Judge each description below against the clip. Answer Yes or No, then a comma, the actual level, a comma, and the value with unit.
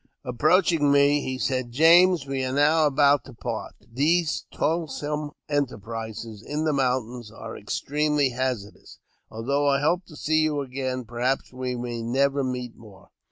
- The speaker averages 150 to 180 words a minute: Yes, average, 155 wpm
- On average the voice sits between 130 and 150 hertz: Yes, low, 135 Hz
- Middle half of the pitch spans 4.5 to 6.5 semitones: No, average, 3.3 semitones